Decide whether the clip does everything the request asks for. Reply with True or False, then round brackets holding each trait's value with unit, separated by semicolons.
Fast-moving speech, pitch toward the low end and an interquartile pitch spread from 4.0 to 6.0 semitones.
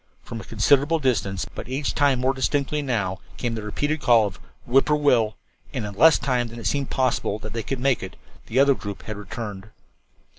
True (210 wpm; 120 Hz; 4.6 semitones)